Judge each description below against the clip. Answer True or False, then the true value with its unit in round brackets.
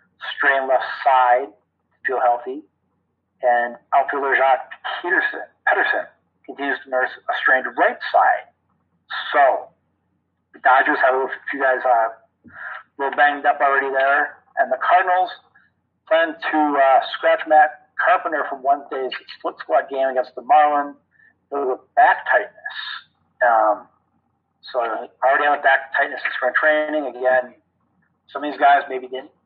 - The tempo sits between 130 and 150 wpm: True (145 wpm)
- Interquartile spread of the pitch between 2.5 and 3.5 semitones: True (3.2 semitones)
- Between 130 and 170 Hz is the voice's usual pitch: True (140 Hz)